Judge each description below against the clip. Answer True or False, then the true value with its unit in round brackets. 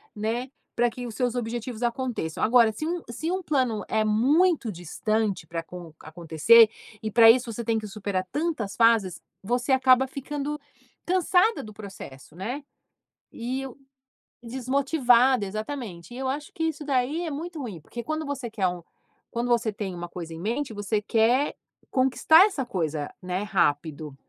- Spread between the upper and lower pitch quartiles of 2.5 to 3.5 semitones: False (4.9 semitones)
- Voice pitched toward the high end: True (235 Hz)